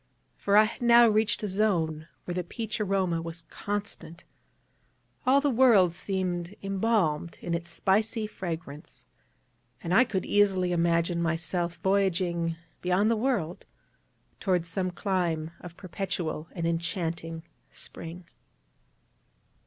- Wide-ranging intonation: No, average, 3.5 semitones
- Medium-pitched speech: Yes, medium, 180 Hz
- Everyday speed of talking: No, slow, 120 wpm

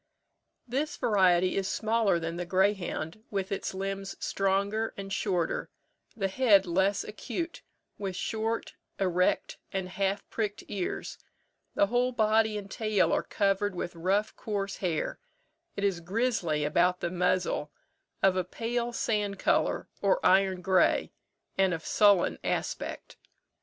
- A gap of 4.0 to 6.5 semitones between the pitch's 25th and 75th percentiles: No, average, 2.7 semitones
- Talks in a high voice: Yes, high, 195 Hz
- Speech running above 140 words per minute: No, slow, 135 wpm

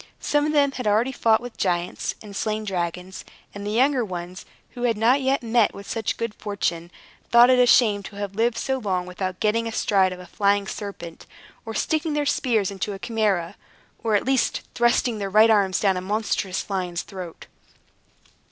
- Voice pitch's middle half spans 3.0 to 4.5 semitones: Yes, average, 3.9 semitones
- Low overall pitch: No, high, 210 Hz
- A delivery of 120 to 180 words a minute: No, average, 190 wpm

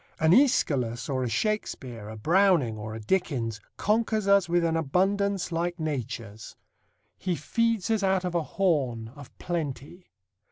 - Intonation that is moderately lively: No, wide, 7.7 semitones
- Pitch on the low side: No, medium, 165 Hz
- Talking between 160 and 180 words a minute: No, average, 150 wpm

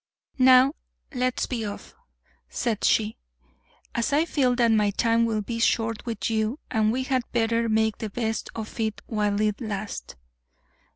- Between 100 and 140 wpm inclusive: No, average, 160 wpm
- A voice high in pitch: Yes, high, 225 Hz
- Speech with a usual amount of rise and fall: No, narrow, 2.3 semitones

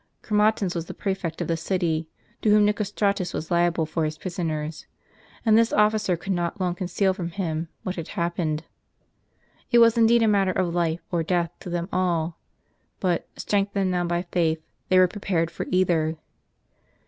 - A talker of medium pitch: Yes, medium, 175 Hz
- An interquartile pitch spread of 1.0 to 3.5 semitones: Yes, average, 2.9 semitones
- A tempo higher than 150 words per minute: Yes, average, 175 wpm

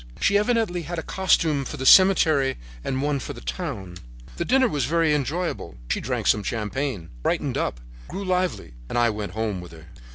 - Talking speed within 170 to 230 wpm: Yes, average, 190 wpm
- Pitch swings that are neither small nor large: No, wide, 8.2 semitones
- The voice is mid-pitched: Yes, medium, 145 Hz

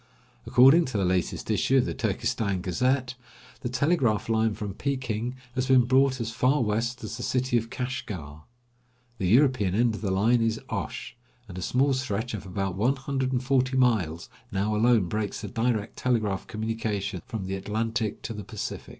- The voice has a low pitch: Yes, low, 115 Hz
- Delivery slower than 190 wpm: Yes, average, 175 wpm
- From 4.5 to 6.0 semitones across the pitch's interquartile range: No, average, 3.8 semitones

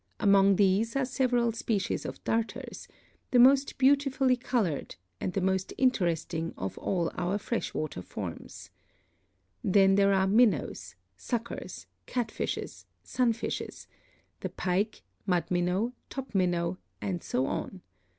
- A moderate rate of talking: No, slow, 120 wpm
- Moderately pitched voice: No, high, 200 Hz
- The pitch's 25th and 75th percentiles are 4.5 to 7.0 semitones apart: Yes, average, 5.2 semitones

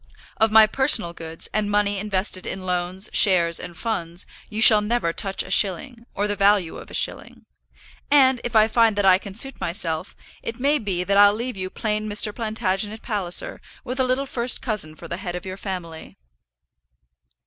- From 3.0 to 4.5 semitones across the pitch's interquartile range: Yes, average, 3.3 semitones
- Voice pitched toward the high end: Yes, high, 205 Hz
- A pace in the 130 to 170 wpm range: No, average, 190 wpm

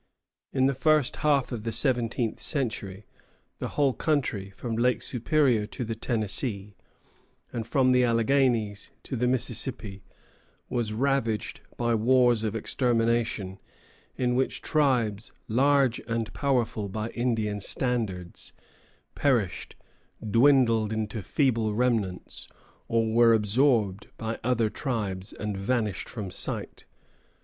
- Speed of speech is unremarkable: No, slow, 120 wpm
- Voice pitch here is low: Yes, low, 115 Hz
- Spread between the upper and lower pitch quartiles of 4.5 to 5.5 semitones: No, average, 3.1 semitones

